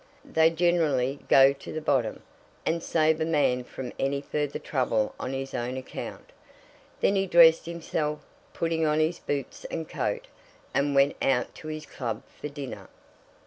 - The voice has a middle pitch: Yes, medium, 150 Hz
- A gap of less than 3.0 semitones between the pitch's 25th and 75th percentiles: No, average, 3.3 semitones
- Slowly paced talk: No, average, 165 wpm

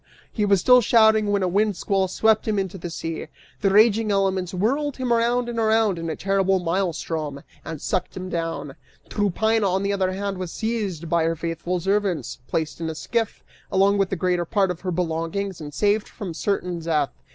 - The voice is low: No, high, 190 Hz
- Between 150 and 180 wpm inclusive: No, average, 195 wpm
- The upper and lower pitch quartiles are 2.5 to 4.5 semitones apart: Yes, average, 3.7 semitones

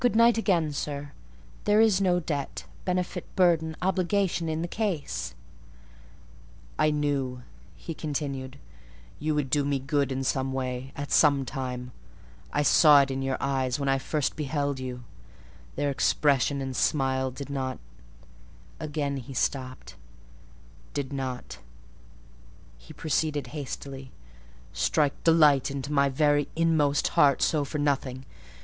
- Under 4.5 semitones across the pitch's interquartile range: Yes, average, 2.7 semitones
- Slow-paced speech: Yes, slow, 130 wpm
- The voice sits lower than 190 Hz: Yes, medium, 140 Hz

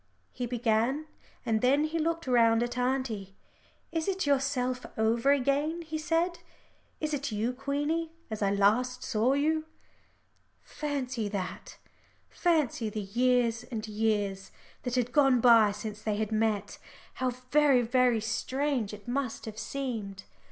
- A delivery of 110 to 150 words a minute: Yes, average, 140 wpm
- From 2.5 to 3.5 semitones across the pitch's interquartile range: No, average, 4.4 semitones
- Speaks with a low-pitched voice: No, very high, 250 Hz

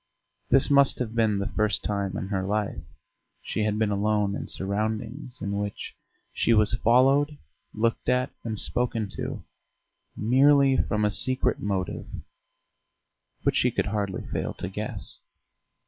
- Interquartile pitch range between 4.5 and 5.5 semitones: No, average, 3.5 semitones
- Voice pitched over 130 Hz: No, low, 110 Hz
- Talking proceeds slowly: No, average, 145 wpm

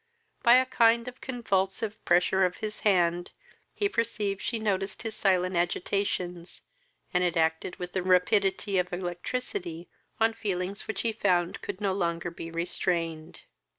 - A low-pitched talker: No, high, 190 Hz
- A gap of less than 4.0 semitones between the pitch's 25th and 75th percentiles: Yes, average, 3.6 semitones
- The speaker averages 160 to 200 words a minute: No, average, 150 wpm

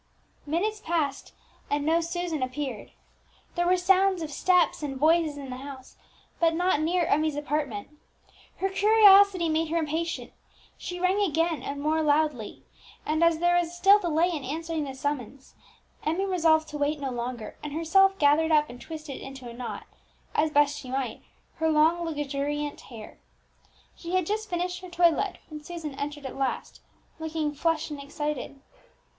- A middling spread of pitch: Yes, average, 3.2 semitones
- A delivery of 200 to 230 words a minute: No, average, 165 wpm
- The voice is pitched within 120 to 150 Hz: No, very high, 315 Hz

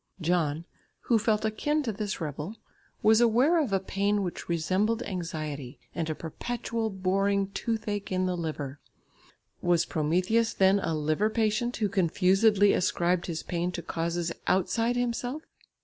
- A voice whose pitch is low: No, high, 195 Hz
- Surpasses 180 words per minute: No, average, 145 wpm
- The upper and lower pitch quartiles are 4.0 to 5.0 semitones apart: Yes, average, 4.5 semitones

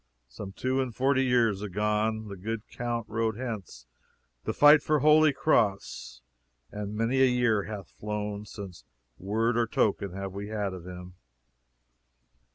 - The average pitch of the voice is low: Yes, low, 105 Hz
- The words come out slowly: No, average, 150 wpm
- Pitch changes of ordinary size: Yes, average, 3.5 semitones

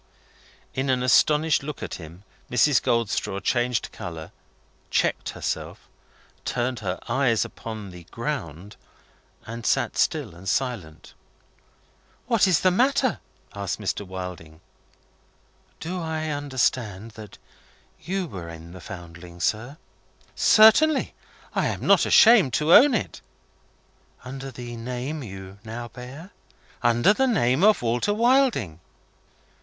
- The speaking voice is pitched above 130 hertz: No, low, 120 Hz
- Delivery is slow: Yes, slow, 120 wpm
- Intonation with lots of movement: Yes, wide, 8.0 semitones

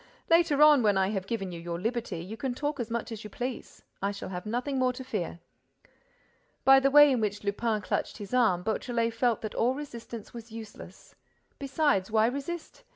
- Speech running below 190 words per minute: No, average, 195 wpm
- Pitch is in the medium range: No, high, 230 Hz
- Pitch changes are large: No, average, 4.3 semitones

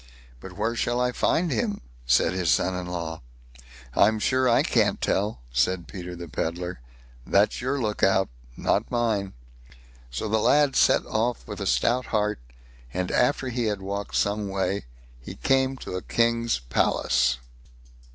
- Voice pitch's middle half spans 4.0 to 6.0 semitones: Yes, average, 4.8 semitones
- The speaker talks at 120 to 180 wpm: Yes, average, 160 wpm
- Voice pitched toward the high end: No, low, 100 Hz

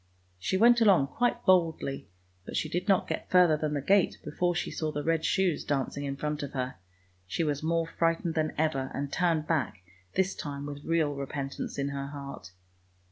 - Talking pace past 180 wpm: Yes, average, 195 wpm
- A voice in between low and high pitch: Yes, medium, 155 Hz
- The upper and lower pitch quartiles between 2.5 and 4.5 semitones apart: Yes, average, 3.5 semitones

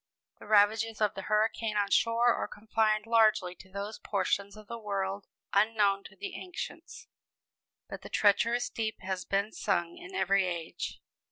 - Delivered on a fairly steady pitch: Yes, narrow, 2.1 semitones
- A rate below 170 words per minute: Yes, average, 160 wpm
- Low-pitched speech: No, high, 210 Hz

